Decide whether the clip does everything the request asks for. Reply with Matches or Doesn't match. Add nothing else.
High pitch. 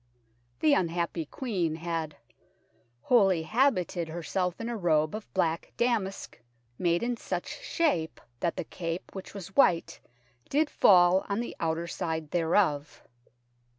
Doesn't match